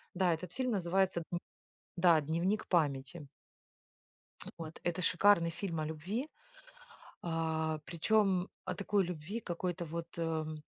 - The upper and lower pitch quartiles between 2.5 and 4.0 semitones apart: Yes, average, 2.9 semitones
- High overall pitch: No, medium, 170 Hz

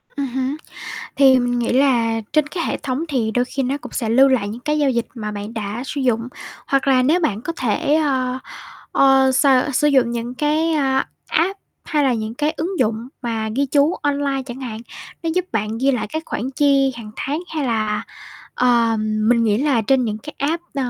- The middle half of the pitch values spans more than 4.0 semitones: No, average, 3.7 semitones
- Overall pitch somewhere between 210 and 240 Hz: No, very high, 260 Hz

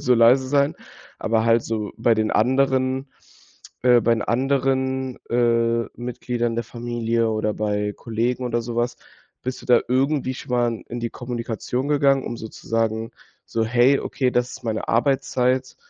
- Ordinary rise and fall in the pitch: No, narrow, 2.1 semitones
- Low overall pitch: Yes, low, 120 Hz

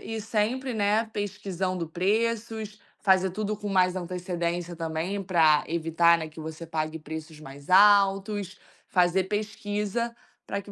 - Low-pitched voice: No, high, 190 Hz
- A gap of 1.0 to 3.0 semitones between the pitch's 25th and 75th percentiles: No, average, 3.7 semitones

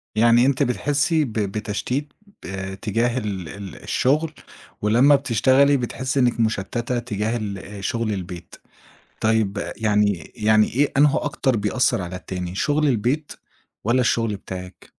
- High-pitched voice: No, low, 115 Hz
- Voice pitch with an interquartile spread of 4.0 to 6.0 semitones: Yes, average, 4.5 semitones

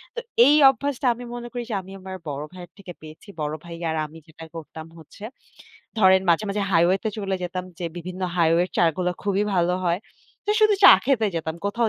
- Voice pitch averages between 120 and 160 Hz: No, medium, 185 Hz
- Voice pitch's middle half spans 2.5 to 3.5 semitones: No, average, 4.0 semitones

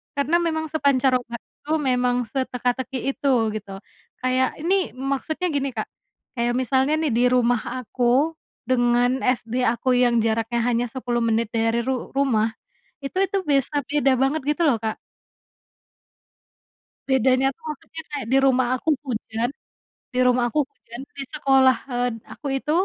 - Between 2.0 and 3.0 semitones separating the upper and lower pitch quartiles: Yes, narrow, 2.6 semitones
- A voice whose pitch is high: Yes, very high, 255 Hz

